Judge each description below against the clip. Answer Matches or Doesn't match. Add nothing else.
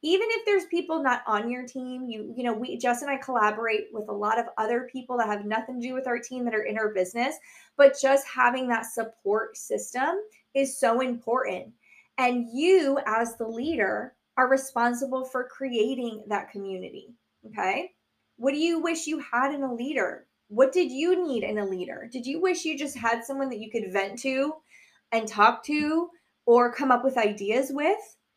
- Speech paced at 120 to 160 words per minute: Doesn't match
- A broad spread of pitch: Doesn't match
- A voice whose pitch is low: Doesn't match